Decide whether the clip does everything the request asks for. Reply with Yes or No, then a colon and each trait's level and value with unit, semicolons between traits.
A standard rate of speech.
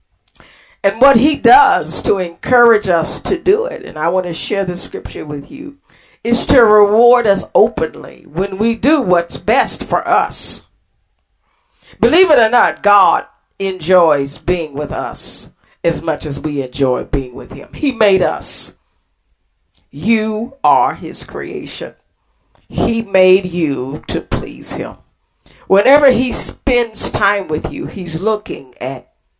Yes: average, 145 wpm